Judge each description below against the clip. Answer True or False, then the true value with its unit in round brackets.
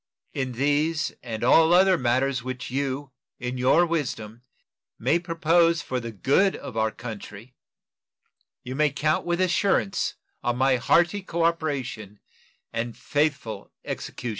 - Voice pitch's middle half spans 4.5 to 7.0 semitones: True (5.3 semitones)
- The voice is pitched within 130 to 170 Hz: True (135 Hz)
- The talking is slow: True (130 wpm)